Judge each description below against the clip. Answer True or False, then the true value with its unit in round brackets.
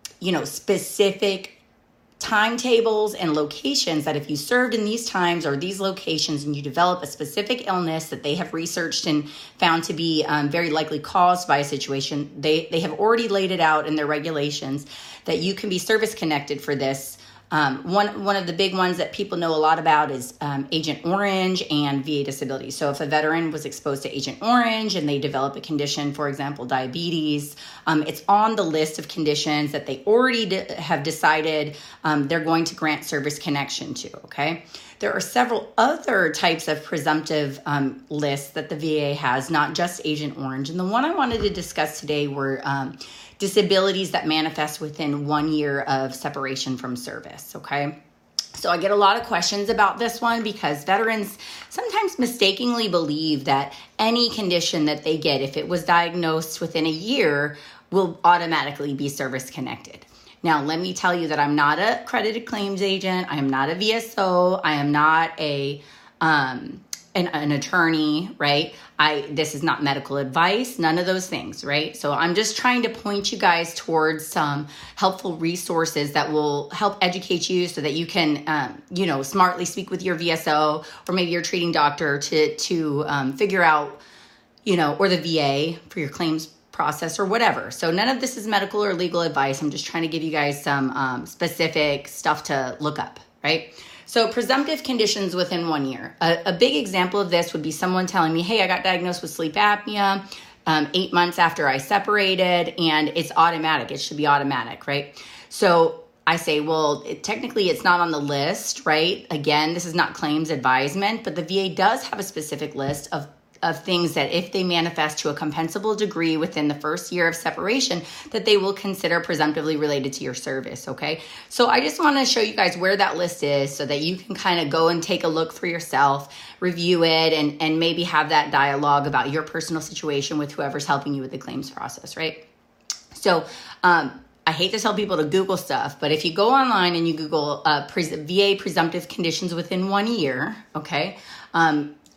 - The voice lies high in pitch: False (160 Hz)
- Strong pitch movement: False (4.1 semitones)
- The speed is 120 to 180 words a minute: False (195 wpm)